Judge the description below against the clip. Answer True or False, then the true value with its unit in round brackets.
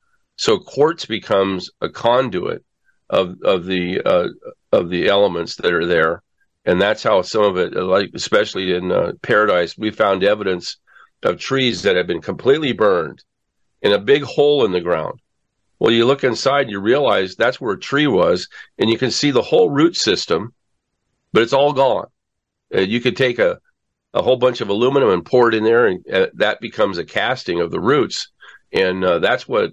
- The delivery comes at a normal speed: True (190 wpm)